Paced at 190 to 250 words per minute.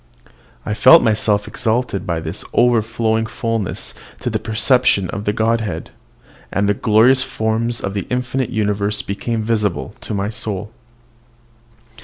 No: slow, 135 wpm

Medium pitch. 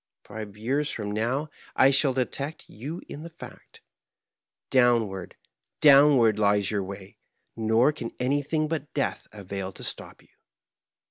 No: low, 120 Hz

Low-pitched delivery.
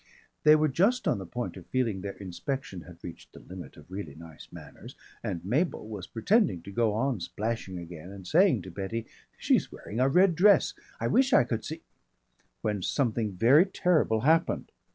Yes: low, 110 Hz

